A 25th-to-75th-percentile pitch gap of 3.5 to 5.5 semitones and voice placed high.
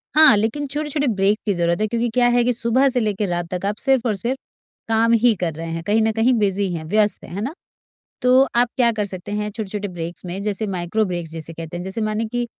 Yes: average, 4.5 semitones; high, 210 Hz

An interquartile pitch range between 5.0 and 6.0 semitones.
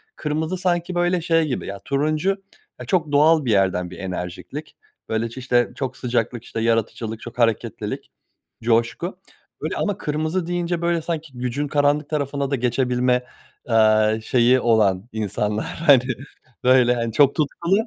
Yes: wide, 5.5 semitones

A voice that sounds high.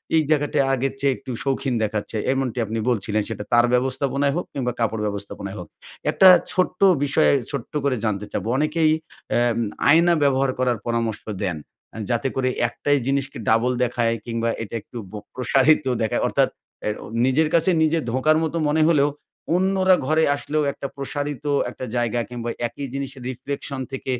No: low, 130 Hz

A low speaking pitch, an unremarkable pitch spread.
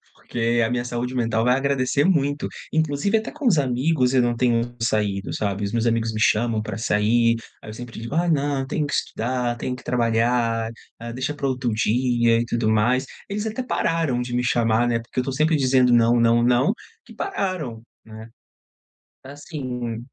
Yes: low, 120 Hz; average, 3.1 semitones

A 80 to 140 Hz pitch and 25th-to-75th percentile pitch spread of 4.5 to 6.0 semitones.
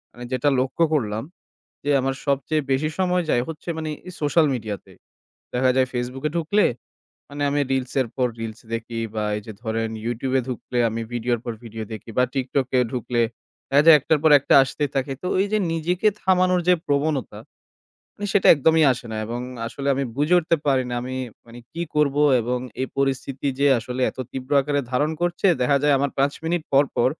No: low, 135 Hz; average, 3.8 semitones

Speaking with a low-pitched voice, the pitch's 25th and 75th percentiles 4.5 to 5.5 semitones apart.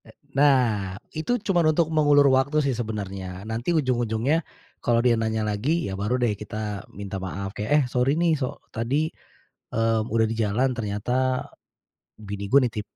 Yes: low, 115 Hz; average, 4.8 semitones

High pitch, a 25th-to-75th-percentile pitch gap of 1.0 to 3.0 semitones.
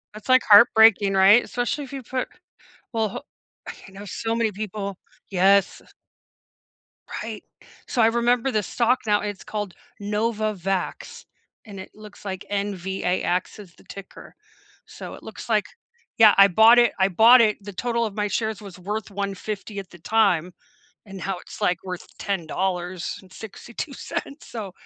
Yes: high, 205 Hz; average, 2.7 semitones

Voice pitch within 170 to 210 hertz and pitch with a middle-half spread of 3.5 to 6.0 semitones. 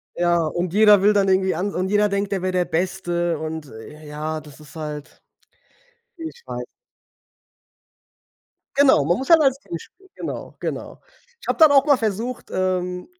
Yes: medium, 185 Hz; average, 4.7 semitones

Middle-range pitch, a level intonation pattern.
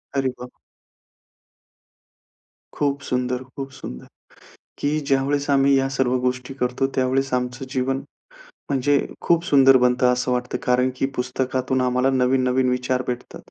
No: low, 130 Hz; narrow, 1.3 semitones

